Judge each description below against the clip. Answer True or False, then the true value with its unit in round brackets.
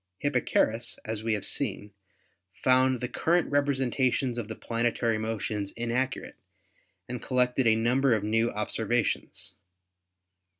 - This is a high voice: False (120 Hz)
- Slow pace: True (120 wpm)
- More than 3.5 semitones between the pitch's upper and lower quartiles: False (2.5 semitones)